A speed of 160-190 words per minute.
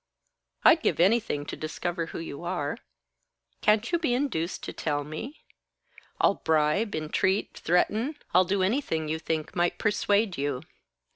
No: average, 145 wpm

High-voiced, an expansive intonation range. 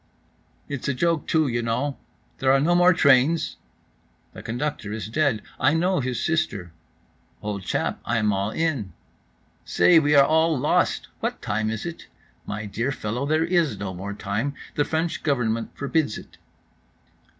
No: low, 135 Hz; wide, 6.5 semitones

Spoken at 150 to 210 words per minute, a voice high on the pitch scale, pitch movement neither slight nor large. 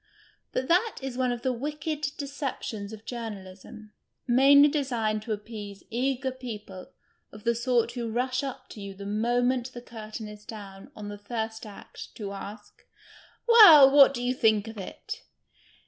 Yes: average, 165 wpm; high, 235 Hz; average, 3.7 semitones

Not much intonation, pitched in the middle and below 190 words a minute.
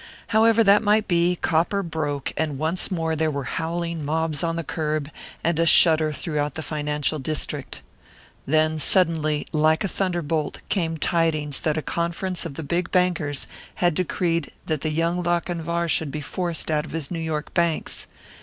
Yes: narrow, 2.2 semitones; medium, 160 Hz; average, 170 wpm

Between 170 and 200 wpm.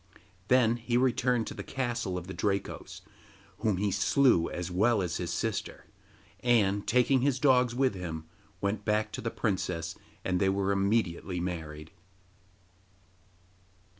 No: average, 140 wpm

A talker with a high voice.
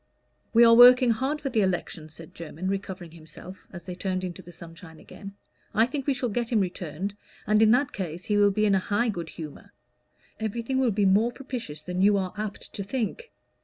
Yes: high, 200 Hz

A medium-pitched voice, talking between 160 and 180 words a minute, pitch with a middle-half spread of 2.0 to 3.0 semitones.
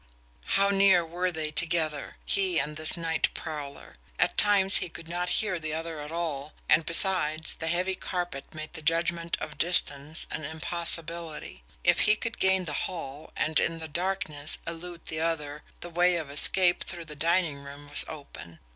Yes: medium, 165 Hz; average, 175 wpm; narrow, 2.5 semitones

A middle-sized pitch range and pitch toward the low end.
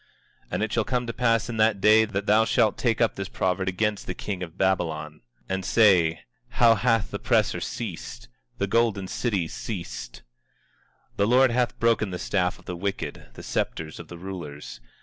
Yes: average, 4.0 semitones; low, 100 Hz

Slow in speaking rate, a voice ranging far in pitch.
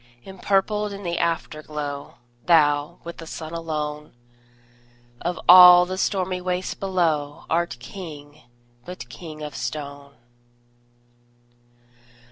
No: slow, 100 wpm; average, 3.4 semitones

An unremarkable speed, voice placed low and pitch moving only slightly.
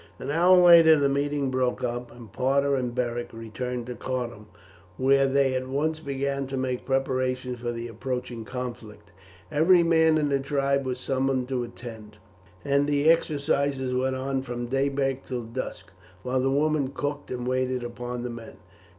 Yes: average, 170 wpm; low, 130 Hz; narrow, 2.3 semitones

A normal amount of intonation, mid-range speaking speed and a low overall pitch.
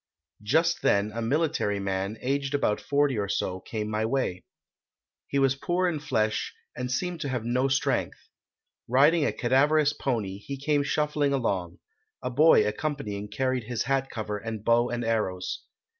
Yes: average, 4.9 semitones; average, 160 wpm; low, 125 Hz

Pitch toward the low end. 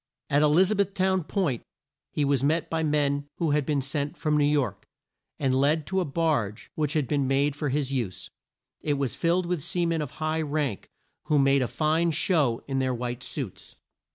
No: medium, 150 Hz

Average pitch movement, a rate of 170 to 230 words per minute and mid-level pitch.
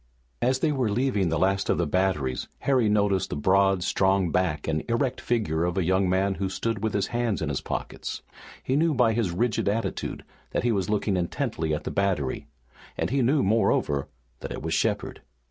No: average, 4.7 semitones; average, 200 wpm; low, 100 Hz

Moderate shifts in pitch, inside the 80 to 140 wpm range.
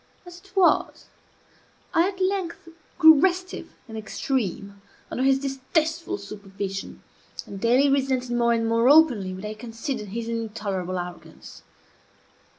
No: wide, 7.1 semitones; slow, 135 wpm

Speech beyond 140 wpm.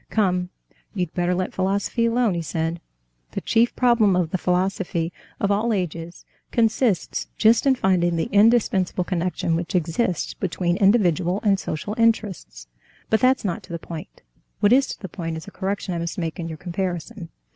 Yes: average, 175 wpm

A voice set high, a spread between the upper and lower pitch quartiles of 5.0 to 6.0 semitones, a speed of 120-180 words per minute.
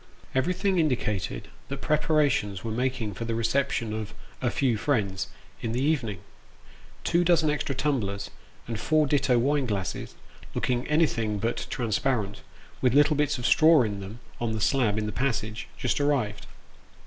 No: low, 125 Hz; average, 5.3 semitones; average, 170 wpm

